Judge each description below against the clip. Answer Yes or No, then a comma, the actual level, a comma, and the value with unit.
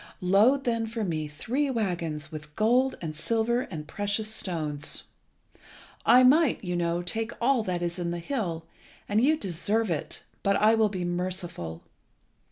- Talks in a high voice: Yes, high, 195 Hz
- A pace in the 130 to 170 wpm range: Yes, average, 160 wpm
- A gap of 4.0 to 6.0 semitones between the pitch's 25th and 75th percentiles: Yes, average, 5.2 semitones